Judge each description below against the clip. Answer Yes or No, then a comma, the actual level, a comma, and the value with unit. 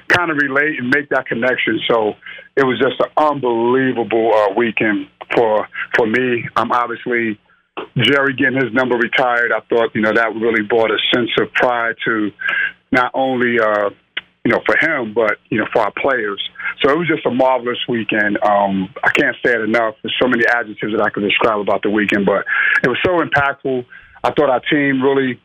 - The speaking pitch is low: Yes, low, 120 Hz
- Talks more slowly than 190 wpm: No, average, 200 wpm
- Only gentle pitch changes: No, average, 3.2 semitones